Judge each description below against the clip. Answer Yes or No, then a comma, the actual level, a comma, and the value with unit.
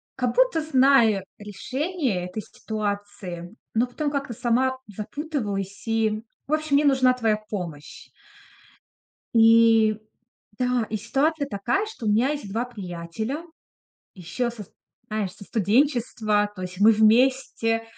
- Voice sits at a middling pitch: No, high, 225 Hz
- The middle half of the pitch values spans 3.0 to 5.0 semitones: Yes, average, 4.3 semitones